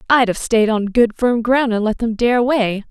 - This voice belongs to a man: No, female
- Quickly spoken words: Yes, fast, 250 wpm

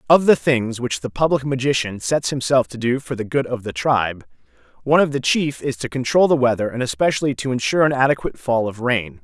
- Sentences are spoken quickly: Yes, fast, 225 wpm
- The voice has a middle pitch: No, low, 125 Hz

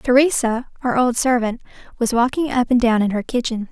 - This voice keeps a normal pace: Yes, average, 195 wpm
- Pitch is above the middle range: Yes, high, 240 Hz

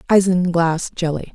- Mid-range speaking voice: Yes, medium, 175 Hz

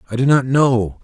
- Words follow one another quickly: Yes, fast, 230 wpm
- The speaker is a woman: No, male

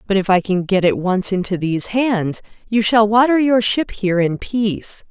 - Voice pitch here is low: No, high, 205 Hz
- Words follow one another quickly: Yes, fast, 210 wpm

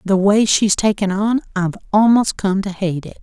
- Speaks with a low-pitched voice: No, high, 200 Hz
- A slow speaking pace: No, fast, 205 wpm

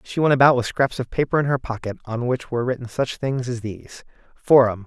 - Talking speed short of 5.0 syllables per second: No, 5.9 syllables/s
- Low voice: Yes, low, 125 Hz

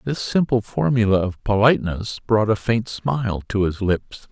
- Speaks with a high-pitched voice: No, low, 110 Hz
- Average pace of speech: Yes, average, 165 wpm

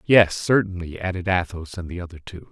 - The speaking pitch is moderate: No, very low, 90 Hz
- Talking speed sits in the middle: Yes, average, 190 wpm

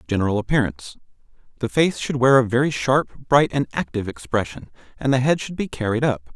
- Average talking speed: Yes, average, 180 wpm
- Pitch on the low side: Yes, low, 125 Hz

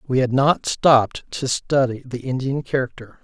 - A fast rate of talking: No, average, 165 wpm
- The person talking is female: No, male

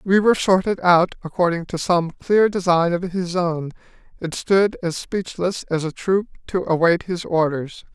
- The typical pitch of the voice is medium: Yes, medium, 175 Hz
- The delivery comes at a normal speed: Yes, average, 175 wpm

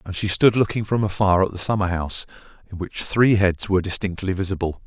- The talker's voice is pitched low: Yes, very low, 95 Hz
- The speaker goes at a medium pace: No, fast, 210 wpm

